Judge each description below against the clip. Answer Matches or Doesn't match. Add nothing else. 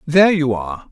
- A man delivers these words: Matches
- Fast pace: Doesn't match